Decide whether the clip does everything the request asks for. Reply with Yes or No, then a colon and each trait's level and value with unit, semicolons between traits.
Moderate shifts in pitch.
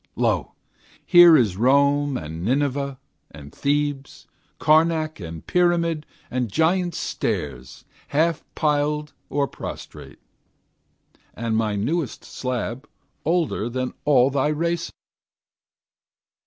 Yes: average, 4.8 semitones